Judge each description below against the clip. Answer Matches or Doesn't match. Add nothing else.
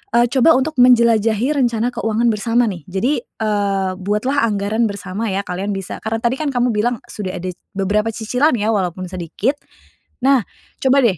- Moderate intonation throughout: Matches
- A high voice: Matches